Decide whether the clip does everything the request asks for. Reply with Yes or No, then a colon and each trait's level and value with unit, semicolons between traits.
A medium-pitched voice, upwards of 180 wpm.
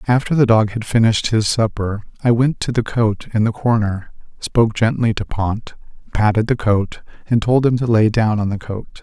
No: low, 110 Hz; fast, 205 wpm